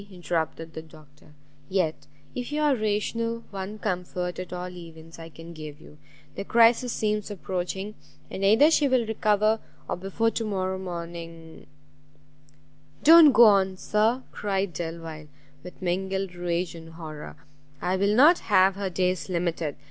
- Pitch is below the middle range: No, medium, 185 Hz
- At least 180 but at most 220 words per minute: No, average, 150 wpm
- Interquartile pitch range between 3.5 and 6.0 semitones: Yes, average, 4.1 semitones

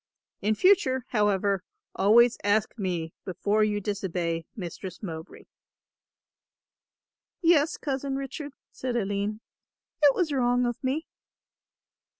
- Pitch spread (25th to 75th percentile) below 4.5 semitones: No, average, 5.2 semitones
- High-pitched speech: Yes, high, 215 Hz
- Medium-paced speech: No, slow, 105 wpm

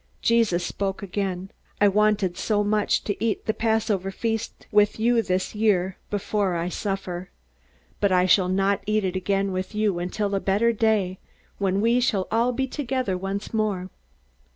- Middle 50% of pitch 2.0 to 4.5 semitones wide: Yes, narrow, 2.6 semitones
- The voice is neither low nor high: No, high, 200 Hz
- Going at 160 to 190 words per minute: Yes, average, 165 wpm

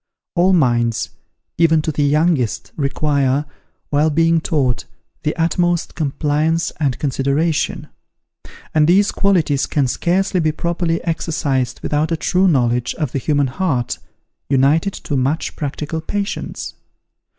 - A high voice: No, medium, 155 Hz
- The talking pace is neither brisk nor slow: No, slow, 125 wpm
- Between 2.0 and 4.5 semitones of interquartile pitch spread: Yes, average, 3.3 semitones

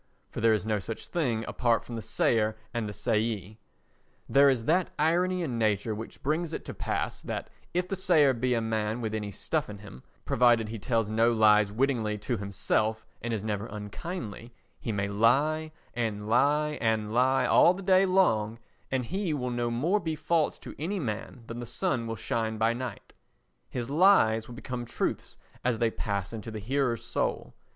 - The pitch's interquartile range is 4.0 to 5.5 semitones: Yes, average, 4.7 semitones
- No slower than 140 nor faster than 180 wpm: No, average, 190 wpm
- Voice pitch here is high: No, low, 115 Hz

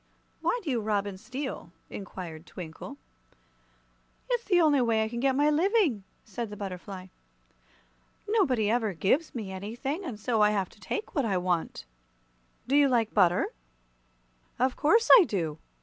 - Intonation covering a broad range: Yes, wide, 6.7 semitones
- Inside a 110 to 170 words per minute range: Yes, average, 160 wpm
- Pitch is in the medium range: No, high, 225 Hz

